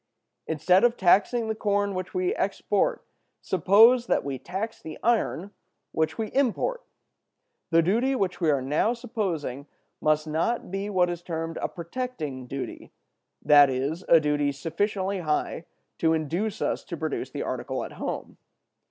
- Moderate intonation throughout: No, wide, 6.0 semitones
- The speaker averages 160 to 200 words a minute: No, average, 150 wpm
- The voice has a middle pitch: Yes, medium, 180 Hz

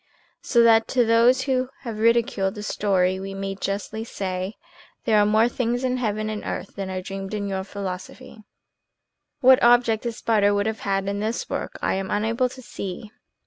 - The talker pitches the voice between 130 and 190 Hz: No, high, 215 Hz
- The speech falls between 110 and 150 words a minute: No, average, 190 wpm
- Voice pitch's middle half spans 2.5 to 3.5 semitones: Yes, average, 3.2 semitones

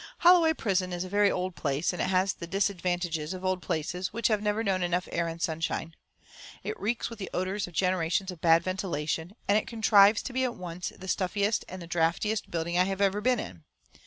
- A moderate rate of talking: No, fast, 220 wpm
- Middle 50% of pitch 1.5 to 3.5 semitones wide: Yes, average, 3.0 semitones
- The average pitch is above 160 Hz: Yes, medium, 185 Hz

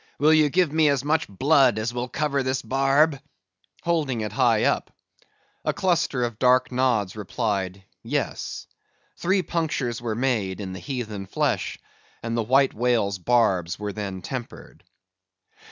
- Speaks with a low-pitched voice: Yes, low, 125 Hz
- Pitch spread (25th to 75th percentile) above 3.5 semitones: Yes, average, 4.8 semitones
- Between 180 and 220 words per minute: No, average, 150 wpm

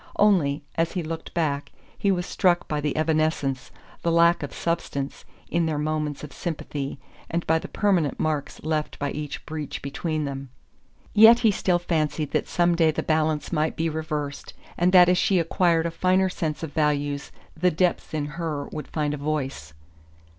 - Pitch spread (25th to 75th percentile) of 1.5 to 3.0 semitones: Yes, narrow, 2.6 semitones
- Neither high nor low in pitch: Yes, medium, 155 Hz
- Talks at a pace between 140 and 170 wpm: No, average, 180 wpm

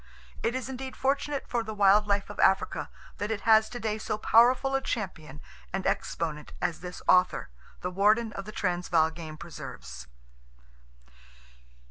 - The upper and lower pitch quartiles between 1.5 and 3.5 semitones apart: No, average, 4.7 semitones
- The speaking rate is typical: Yes, average, 150 wpm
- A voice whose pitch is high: Yes, high, 205 Hz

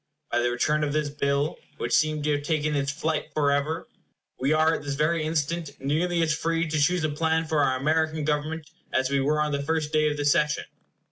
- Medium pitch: Yes, medium, 150 Hz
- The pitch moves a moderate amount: No, narrow, 1.8 semitones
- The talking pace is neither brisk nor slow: No, fast, 220 wpm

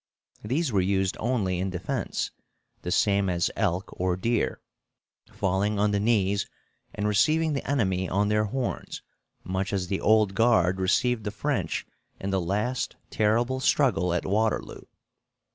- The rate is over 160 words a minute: No, average, 145 wpm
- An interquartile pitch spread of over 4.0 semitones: No, average, 3.6 semitones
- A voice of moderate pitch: No, low, 105 Hz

